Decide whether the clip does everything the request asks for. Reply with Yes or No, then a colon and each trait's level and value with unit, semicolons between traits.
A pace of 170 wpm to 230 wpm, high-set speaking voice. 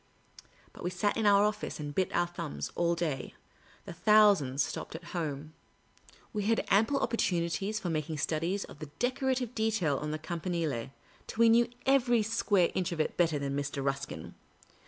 No: average, 175 wpm; medium, 175 Hz